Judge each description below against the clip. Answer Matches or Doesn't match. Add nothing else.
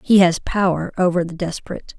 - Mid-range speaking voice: Matches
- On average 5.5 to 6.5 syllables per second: Matches